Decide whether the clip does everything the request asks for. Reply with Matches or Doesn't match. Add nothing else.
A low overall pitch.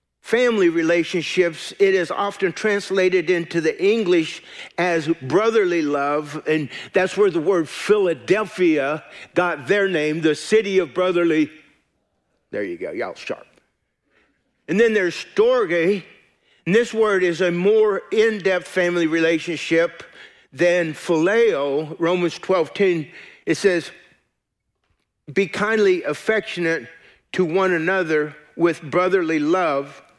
Doesn't match